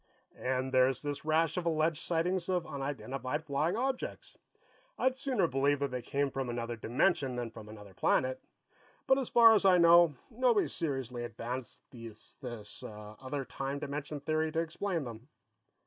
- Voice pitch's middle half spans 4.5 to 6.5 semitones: Yes, average, 5.0 semitones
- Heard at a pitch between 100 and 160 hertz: Yes, medium, 140 Hz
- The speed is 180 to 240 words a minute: No, average, 155 wpm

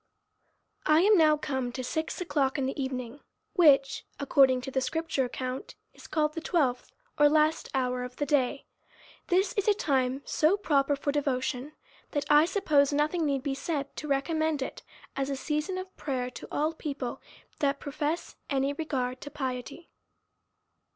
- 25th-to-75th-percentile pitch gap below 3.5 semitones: Yes, average, 2.8 semitones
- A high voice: Yes, very high, 285 Hz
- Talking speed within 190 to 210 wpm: No, average, 170 wpm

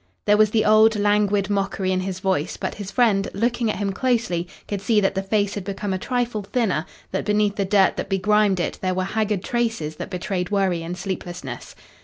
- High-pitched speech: Yes, high, 200 Hz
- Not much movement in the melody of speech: Yes, narrow, 2.2 semitones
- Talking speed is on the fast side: Yes, fast, 210 wpm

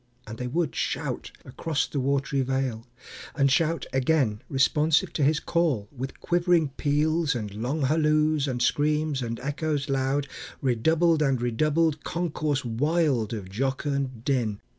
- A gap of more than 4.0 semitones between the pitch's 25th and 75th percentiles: No, average, 3.4 semitones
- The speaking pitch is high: No, medium, 140 Hz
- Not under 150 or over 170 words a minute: No, average, 140 wpm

